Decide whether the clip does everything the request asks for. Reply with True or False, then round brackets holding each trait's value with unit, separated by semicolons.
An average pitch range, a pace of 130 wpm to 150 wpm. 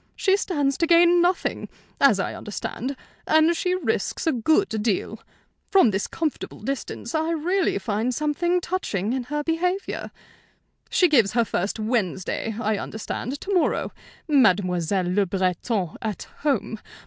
False (8.2 semitones; 140 wpm)